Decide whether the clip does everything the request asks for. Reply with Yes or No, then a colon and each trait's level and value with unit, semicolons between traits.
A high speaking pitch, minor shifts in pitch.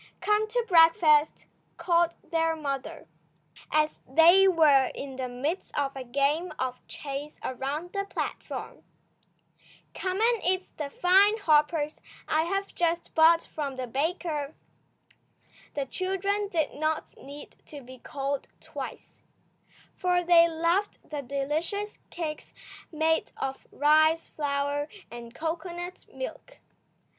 No: very high, 315 Hz; average, 3.9 semitones